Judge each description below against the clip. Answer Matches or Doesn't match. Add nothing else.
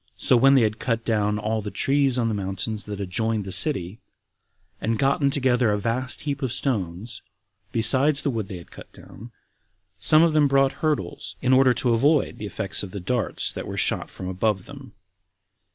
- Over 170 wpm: Matches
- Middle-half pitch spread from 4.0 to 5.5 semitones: Matches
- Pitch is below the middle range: Matches